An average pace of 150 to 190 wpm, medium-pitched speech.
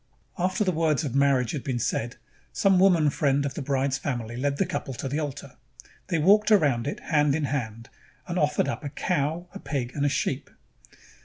No: fast, 205 wpm; medium, 145 Hz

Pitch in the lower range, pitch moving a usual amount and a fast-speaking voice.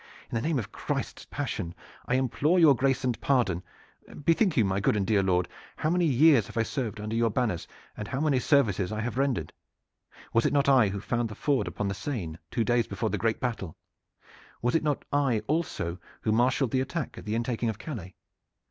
Yes: low, 120 Hz; average, 4.8 semitones; fast, 210 wpm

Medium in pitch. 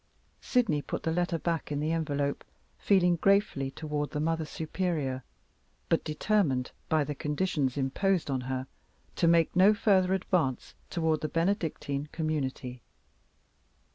Yes: medium, 155 Hz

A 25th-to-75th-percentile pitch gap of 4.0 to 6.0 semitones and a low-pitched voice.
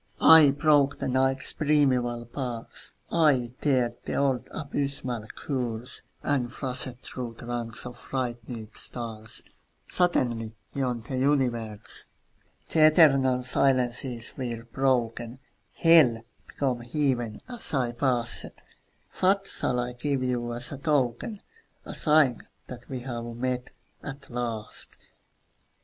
No: average, 2.7 semitones; low, 125 Hz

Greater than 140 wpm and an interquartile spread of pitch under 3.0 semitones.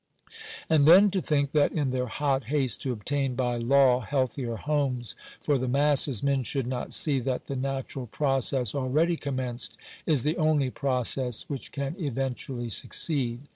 Yes: average, 160 wpm; narrow, 2.4 semitones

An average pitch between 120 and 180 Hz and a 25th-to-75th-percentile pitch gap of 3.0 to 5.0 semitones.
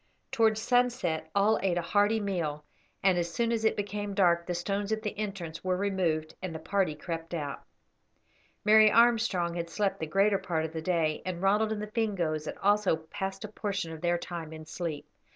No: high, 190 Hz; average, 4.0 semitones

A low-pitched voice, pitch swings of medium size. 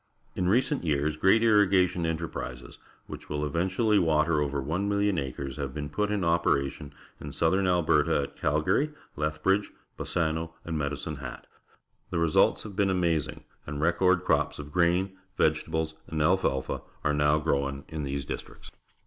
Yes: very low, 80 Hz; average, 4.1 semitones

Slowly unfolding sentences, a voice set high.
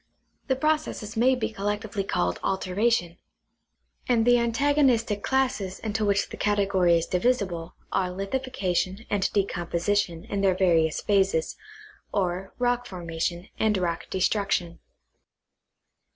Yes: slow, 125 wpm; high, 200 Hz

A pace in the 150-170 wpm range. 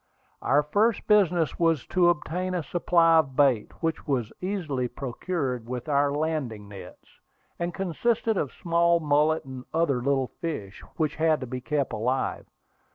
Yes: average, 155 wpm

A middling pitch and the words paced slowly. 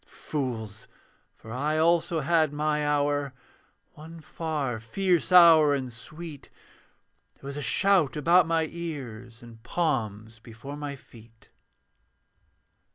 Yes: medium, 145 Hz; slow, 115 wpm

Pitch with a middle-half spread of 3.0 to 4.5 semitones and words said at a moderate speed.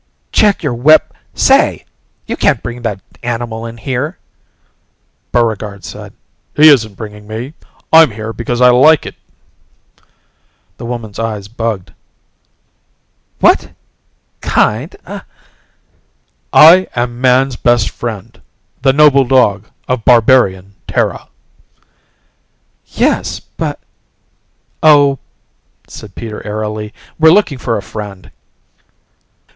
No: average, 3.7 semitones; slow, 110 wpm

